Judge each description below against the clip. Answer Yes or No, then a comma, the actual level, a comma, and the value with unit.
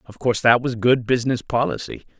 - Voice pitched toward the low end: Yes, low, 120 Hz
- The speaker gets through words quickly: No, average, 190 wpm